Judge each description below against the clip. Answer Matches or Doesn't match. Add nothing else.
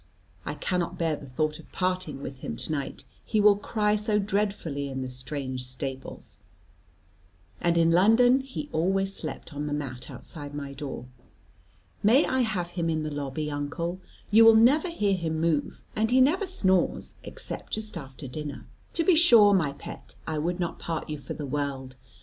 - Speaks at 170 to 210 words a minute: Matches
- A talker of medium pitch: Matches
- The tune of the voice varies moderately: Doesn't match